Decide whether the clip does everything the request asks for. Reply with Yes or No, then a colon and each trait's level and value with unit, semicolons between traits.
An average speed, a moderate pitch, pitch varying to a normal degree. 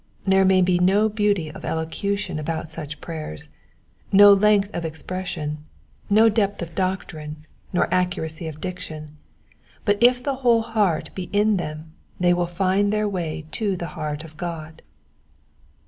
Yes: average, 150 wpm; medium, 180 Hz; average, 4.2 semitones